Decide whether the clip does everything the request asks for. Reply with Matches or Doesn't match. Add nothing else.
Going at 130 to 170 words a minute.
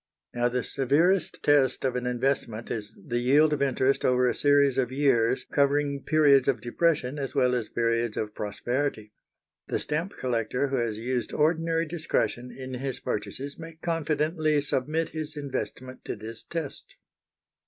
Matches